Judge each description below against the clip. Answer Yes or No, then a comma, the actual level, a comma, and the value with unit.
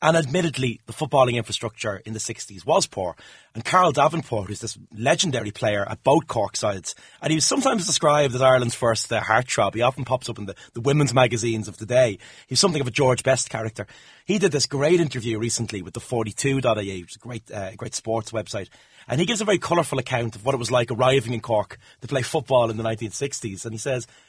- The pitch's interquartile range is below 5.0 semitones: Yes, average, 3.7 semitones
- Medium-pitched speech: No, low, 120 Hz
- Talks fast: Yes, fast, 225 wpm